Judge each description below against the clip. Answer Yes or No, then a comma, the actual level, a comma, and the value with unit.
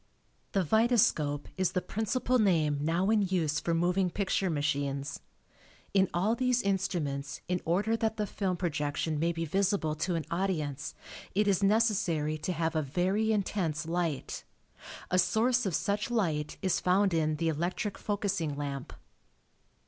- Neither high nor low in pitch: Yes, medium, 180 Hz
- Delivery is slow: No, average, 150 wpm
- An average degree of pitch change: Yes, average, 4.6 semitones